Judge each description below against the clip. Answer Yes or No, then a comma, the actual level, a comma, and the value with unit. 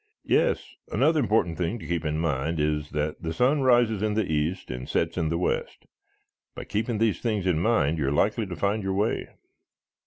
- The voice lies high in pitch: No, very low, 90 Hz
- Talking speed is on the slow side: No, fast, 205 wpm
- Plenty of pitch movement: Yes, wide, 5.8 semitones